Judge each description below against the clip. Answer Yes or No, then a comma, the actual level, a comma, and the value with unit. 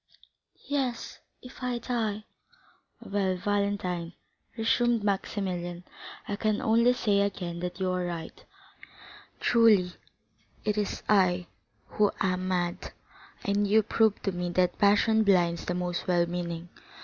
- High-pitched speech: Yes, high, 200 Hz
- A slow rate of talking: Yes, slow, 125 wpm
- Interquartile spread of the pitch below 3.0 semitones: No, average, 3.3 semitones